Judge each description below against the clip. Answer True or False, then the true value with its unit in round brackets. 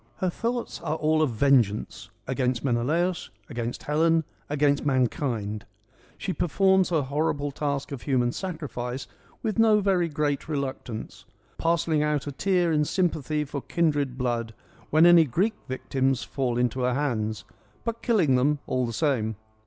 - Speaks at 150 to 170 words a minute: True (155 wpm)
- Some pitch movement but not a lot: True (4.6 semitones)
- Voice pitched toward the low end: False (145 Hz)